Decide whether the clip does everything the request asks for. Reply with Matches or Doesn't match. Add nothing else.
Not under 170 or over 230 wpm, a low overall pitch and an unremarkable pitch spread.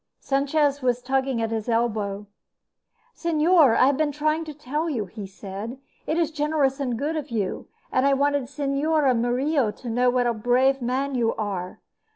Doesn't match